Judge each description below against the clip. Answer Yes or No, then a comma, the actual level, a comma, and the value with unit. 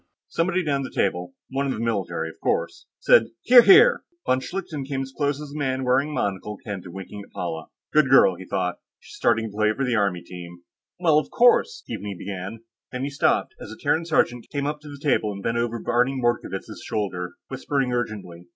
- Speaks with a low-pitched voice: Yes, low, 120 Hz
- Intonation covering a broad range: Yes, wide, 6.4 semitones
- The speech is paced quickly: Yes, fast, 210 wpm